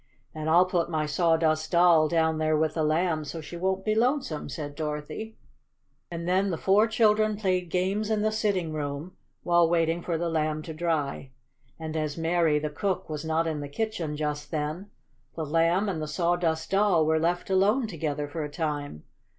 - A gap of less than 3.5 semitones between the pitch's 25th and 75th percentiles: Yes, average, 3.1 semitones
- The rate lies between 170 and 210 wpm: Yes, average, 190 wpm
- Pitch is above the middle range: No, medium, 165 Hz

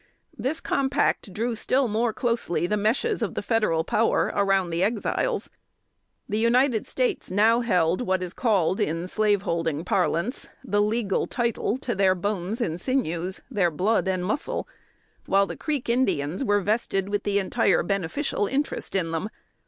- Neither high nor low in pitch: No, high, 205 Hz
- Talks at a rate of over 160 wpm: No, average, 155 wpm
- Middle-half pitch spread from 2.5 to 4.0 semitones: No, average, 4.4 semitones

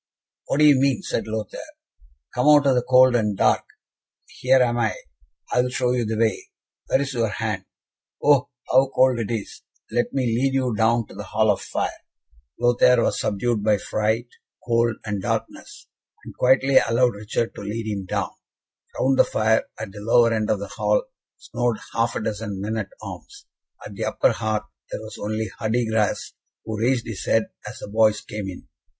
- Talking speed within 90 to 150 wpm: No, average, 185 wpm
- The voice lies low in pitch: Yes, low, 115 Hz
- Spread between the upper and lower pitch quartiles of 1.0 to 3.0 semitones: Yes, average, 2.7 semitones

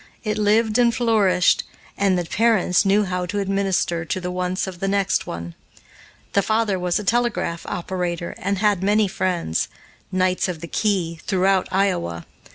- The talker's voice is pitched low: No, high, 190 Hz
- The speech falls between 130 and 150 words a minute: No, average, 165 wpm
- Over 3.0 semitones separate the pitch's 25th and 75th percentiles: No, narrow, 2.5 semitones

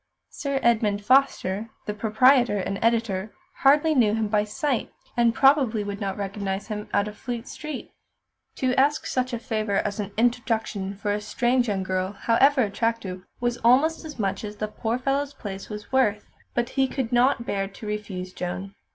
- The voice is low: No, high, 220 Hz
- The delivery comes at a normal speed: Yes, average, 175 wpm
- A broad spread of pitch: No, average, 3.8 semitones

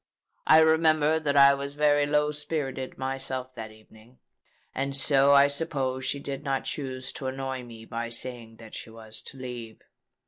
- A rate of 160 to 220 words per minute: Yes, average, 170 wpm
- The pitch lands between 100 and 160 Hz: Yes, low, 135 Hz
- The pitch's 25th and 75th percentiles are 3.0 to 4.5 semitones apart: No, narrow, 2.6 semitones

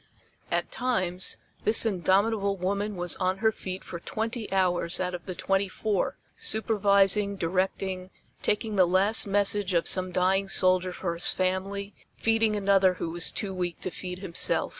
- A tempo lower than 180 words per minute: Yes, average, 160 wpm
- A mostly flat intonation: Yes, narrow, 1.9 semitones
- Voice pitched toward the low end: No, high, 190 Hz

